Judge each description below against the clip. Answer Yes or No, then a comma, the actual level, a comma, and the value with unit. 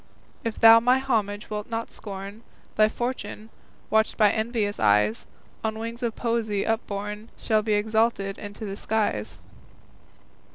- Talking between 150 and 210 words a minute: No, slow, 135 wpm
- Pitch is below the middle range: No, high, 220 Hz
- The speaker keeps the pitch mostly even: Yes, narrow, 1.9 semitones